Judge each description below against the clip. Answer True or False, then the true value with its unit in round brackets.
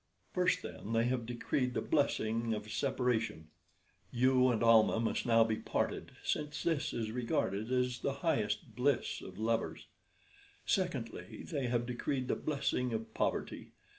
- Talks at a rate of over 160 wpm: False (145 wpm)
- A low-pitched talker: True (120 Hz)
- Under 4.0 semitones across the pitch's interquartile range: True (2.4 semitones)